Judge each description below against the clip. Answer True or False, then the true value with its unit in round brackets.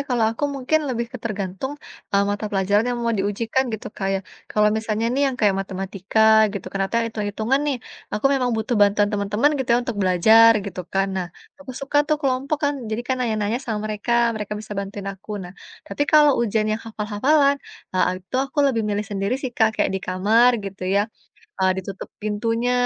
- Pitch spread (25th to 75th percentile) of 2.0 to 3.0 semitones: False (3.7 semitones)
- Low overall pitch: False (215 Hz)